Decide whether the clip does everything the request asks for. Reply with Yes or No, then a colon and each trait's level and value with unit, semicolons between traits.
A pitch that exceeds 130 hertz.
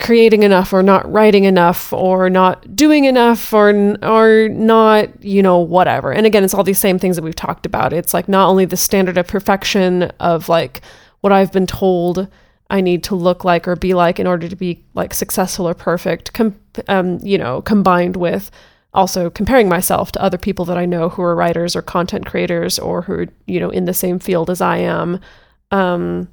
Yes: medium, 185 Hz